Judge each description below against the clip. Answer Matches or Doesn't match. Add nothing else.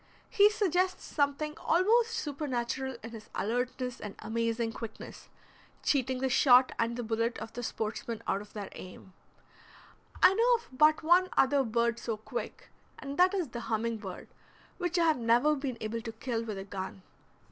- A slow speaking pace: Doesn't match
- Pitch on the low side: Doesn't match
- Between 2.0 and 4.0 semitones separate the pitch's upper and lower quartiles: Doesn't match